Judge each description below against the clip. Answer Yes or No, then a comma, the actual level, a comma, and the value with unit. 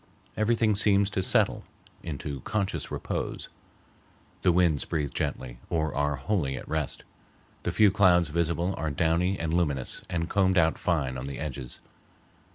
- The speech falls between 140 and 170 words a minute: Yes, average, 150 wpm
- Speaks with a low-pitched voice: Yes, very low, 85 Hz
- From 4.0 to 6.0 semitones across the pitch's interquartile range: Yes, average, 4.5 semitones